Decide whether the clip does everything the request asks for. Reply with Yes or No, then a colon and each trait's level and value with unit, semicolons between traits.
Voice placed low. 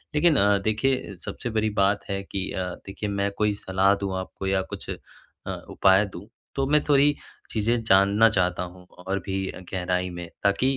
Yes: low, 100 Hz